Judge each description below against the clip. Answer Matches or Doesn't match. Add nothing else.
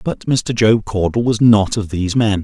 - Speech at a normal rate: Doesn't match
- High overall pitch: Doesn't match